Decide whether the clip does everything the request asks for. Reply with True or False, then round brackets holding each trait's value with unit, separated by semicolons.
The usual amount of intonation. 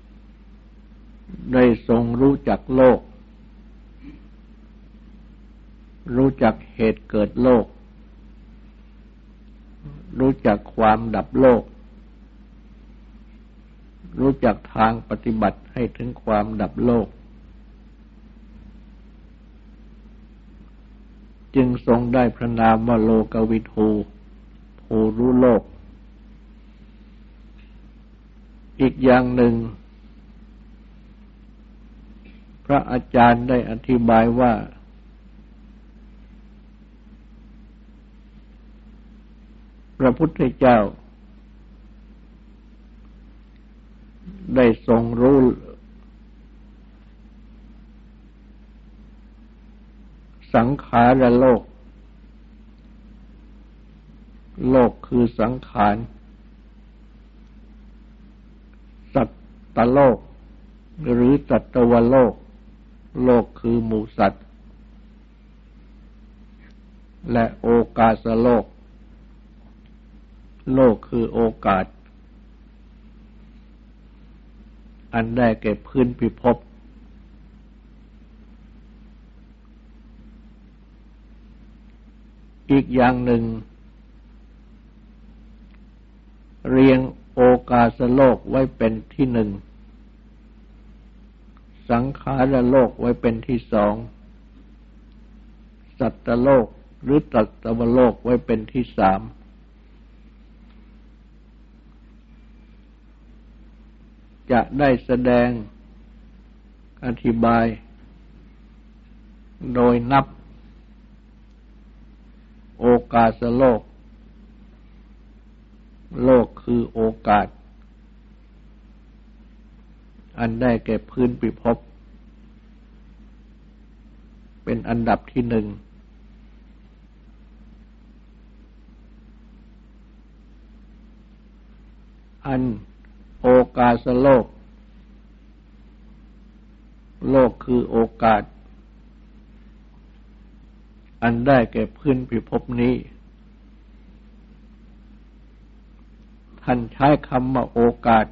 True (3.9 semitones)